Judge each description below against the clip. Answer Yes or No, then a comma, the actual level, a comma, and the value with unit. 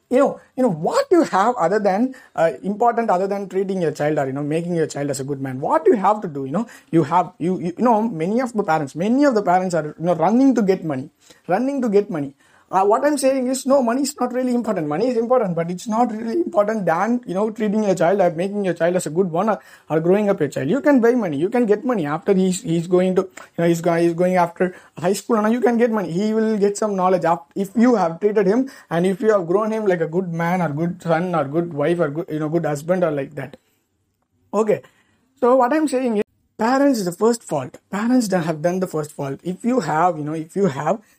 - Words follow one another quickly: Yes, fast, 270 wpm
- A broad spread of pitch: Yes, wide, 5.7 semitones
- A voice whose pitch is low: No, medium, 185 Hz